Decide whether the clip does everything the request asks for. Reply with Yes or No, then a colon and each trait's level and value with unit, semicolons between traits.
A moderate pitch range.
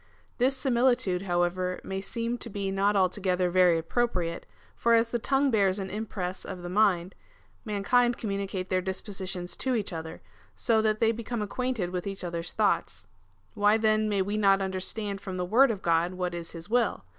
Yes: average, 3.6 semitones